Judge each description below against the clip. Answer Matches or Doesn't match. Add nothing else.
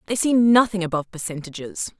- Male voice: Doesn't match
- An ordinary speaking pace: Matches